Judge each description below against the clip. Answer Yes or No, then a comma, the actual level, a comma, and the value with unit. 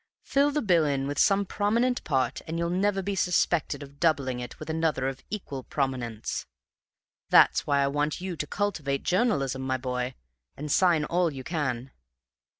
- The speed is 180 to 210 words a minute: No, average, 165 wpm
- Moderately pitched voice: Yes, medium, 150 Hz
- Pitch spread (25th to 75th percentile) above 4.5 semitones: Yes, average, 5.3 semitones